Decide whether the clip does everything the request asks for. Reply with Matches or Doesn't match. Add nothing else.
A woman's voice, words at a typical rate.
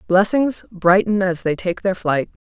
Matches